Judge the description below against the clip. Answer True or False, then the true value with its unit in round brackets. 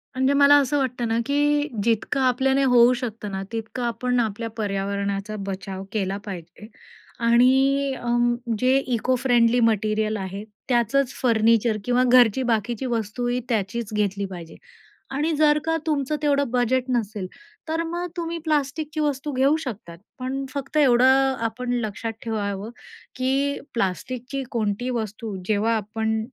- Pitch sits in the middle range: False (240 Hz)